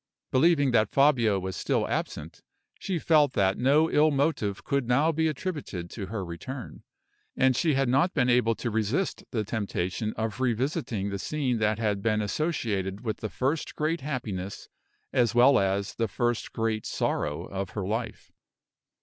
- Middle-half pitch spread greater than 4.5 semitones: Yes, wide, 5.6 semitones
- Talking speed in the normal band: Yes, average, 165 wpm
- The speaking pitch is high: No, low, 115 Hz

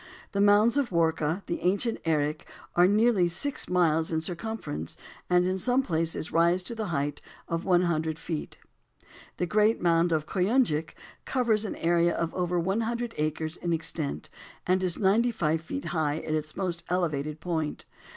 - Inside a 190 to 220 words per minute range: No, average, 170 wpm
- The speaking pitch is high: No, medium, 175 Hz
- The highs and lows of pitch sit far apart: No, average, 4.2 semitones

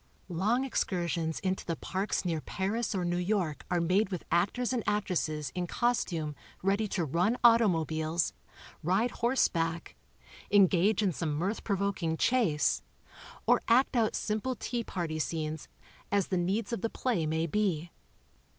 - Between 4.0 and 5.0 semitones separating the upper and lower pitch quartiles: Yes, average, 4.7 semitones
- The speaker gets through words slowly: No, average, 150 wpm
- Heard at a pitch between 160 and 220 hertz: Yes, medium, 185 Hz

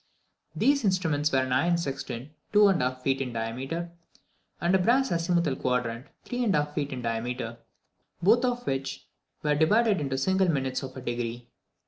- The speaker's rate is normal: Yes, average, 150 wpm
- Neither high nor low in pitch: Yes, medium, 145 Hz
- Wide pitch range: Yes, wide, 6.4 semitones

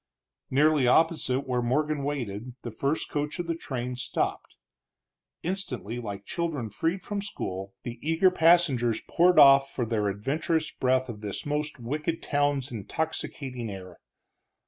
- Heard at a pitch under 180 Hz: Yes, low, 135 Hz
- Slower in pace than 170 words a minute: Yes, average, 140 wpm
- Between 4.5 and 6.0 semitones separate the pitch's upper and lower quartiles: Yes, average, 4.9 semitones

